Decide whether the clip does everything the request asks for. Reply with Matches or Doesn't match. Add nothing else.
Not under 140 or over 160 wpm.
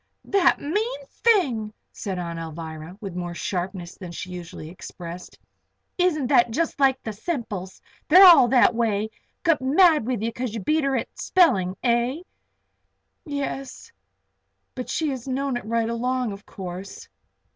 Matches